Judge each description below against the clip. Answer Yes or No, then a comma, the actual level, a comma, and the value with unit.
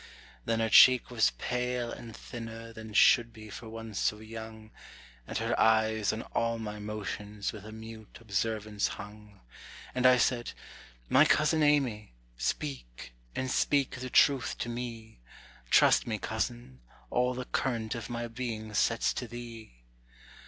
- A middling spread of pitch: No, narrow, 2.1 semitones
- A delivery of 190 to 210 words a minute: No, average, 150 wpm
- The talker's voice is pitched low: Yes, low, 115 Hz